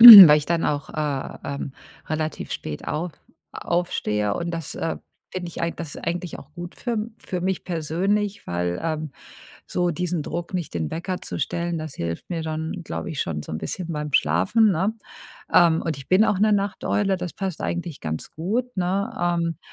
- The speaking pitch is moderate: Yes, medium, 170 Hz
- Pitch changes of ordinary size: Yes, average, 3.4 semitones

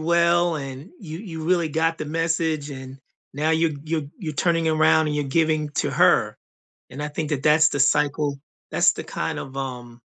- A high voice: No, medium, 155 Hz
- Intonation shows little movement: Yes, narrow, 2.3 semitones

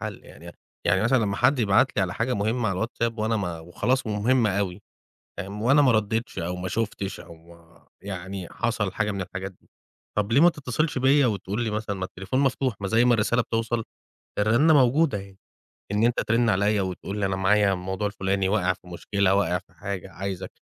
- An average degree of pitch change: Yes, average, 3.5 semitones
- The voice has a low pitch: Yes, low, 105 Hz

